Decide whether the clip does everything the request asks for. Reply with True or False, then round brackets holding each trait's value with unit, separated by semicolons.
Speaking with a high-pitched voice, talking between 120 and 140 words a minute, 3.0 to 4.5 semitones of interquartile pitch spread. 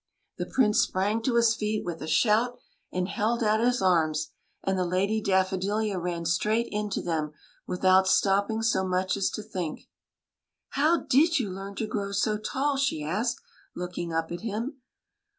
False (200 Hz; 175 wpm; 3.5 semitones)